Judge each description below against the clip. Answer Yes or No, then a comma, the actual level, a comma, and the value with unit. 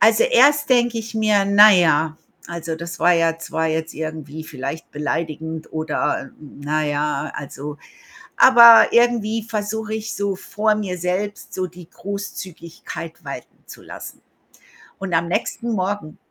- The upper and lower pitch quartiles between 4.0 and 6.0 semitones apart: Yes, average, 5.0 semitones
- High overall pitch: No, medium, 180 Hz